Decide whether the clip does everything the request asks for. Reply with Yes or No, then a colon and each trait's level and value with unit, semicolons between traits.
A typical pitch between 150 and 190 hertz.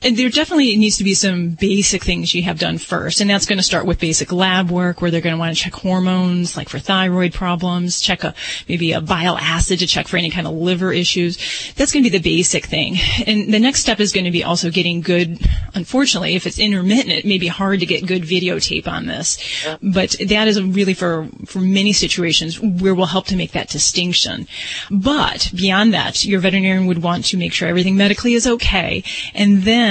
Yes: medium, 185 Hz